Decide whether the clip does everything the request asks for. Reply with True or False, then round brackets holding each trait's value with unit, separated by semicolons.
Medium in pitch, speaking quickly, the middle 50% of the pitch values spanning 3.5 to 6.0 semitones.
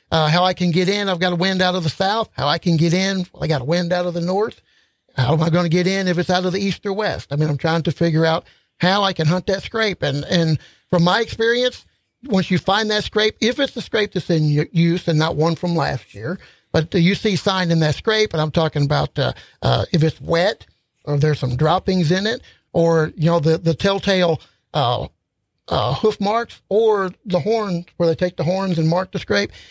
False (180 Hz; 250 wpm; 3.0 semitones)